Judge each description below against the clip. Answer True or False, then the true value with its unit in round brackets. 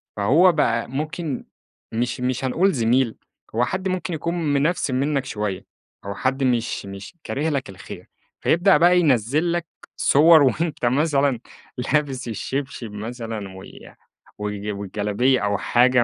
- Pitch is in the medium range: False (130 Hz)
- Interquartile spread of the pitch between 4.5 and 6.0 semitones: True (5.2 semitones)